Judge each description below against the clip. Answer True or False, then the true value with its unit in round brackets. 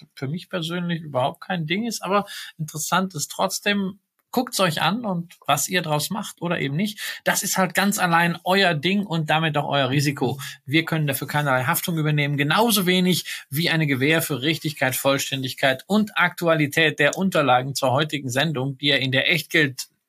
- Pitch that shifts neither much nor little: True (4.0 semitones)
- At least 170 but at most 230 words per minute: True (185 wpm)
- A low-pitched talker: False (165 Hz)